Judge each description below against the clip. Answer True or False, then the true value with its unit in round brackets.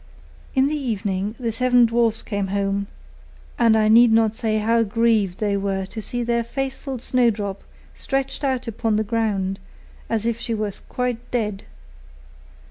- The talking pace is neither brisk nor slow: True (155 wpm)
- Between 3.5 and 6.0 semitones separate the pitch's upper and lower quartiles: False (2.8 semitones)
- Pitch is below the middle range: False (225 Hz)